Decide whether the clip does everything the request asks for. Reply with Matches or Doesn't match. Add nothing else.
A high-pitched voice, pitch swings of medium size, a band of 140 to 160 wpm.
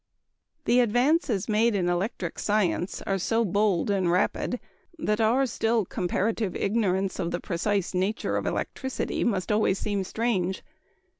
Matches